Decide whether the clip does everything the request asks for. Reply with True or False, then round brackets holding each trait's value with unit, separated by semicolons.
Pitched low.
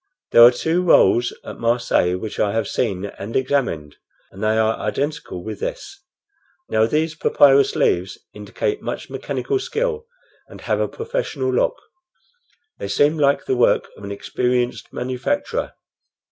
True (125 Hz)